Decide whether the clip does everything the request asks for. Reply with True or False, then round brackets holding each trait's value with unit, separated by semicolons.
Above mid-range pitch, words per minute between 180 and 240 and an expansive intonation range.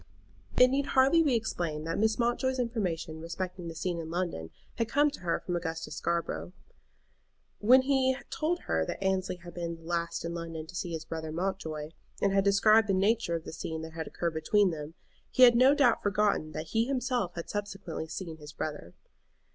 False (180 Hz; 195 wpm; 5.7 semitones)